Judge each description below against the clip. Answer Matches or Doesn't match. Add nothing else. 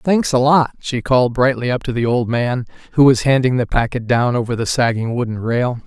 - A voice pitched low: Matches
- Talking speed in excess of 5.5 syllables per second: Doesn't match